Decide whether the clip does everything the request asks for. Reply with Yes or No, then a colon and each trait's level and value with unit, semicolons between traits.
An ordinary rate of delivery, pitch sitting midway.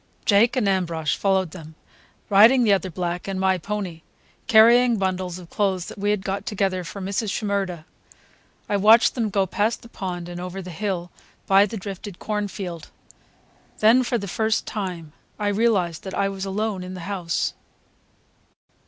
No: average, 170 wpm; high, 195 Hz